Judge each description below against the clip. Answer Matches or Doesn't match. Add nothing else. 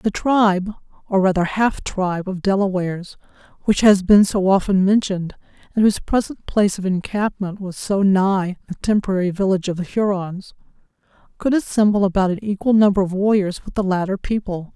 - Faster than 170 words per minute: Doesn't match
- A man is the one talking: Doesn't match